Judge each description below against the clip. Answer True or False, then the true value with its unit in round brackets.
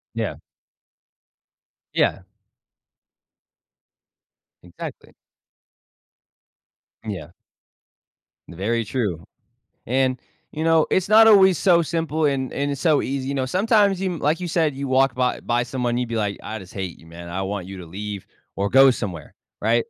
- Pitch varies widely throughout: True (7.7 semitones)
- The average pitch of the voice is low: True (130 Hz)